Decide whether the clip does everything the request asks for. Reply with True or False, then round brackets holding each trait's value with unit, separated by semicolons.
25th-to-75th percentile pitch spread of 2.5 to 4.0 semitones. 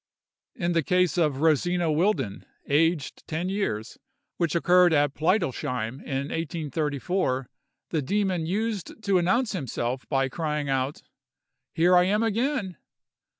False (4.5 semitones)